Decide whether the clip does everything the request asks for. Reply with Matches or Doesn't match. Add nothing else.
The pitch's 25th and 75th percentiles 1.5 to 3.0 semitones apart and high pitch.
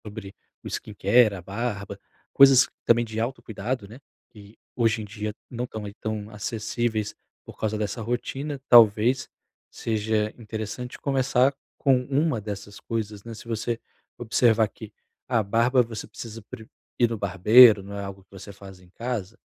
Doesn't match